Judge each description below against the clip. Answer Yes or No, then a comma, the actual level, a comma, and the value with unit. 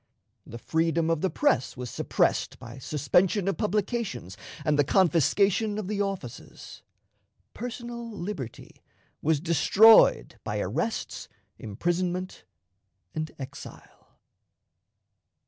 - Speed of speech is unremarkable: No, slow, 100 wpm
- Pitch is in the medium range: Yes, medium, 175 Hz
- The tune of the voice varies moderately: No, wide, 6.2 semitones